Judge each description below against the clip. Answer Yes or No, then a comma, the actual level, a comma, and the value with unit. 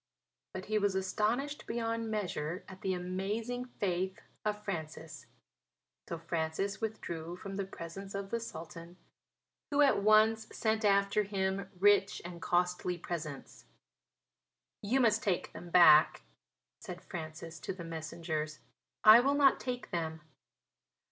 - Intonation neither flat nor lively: Yes, average, 4.1 semitones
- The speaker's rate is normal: No, slow, 130 wpm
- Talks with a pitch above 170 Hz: Yes, high, 190 Hz